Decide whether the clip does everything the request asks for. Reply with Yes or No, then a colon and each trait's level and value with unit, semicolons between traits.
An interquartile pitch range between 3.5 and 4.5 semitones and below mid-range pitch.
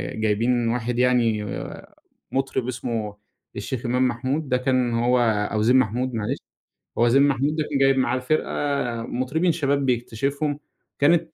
No: average, 2.7 semitones; low, 125 Hz